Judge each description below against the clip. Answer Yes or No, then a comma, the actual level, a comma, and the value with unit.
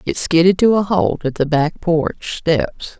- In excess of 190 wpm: Yes, average, 200 wpm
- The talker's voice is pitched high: No, medium, 165 Hz